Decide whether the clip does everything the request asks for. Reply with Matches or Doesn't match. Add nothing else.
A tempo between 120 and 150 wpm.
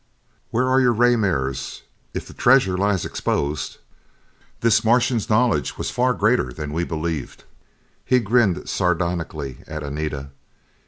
Matches